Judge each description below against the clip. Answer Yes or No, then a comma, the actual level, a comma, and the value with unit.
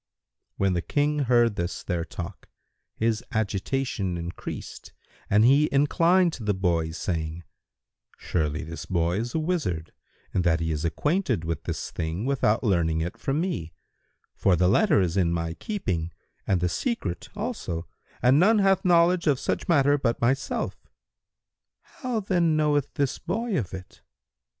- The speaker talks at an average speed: Yes, average, 155 wpm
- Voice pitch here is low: Yes, low, 110 Hz